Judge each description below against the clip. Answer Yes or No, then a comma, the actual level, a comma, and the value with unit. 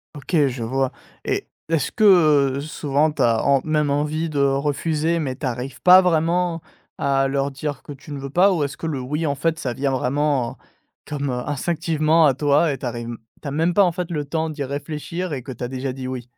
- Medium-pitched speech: Yes, medium, 145 Hz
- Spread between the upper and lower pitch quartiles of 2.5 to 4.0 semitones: Yes, average, 3.0 semitones